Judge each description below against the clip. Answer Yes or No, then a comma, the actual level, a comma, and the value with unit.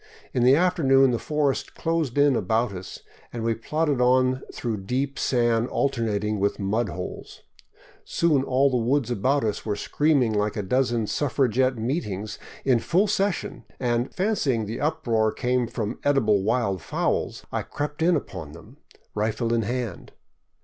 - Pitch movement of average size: Yes, average, 4.2 semitones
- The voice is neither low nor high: No, low, 125 Hz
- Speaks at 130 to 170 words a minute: Yes, average, 155 wpm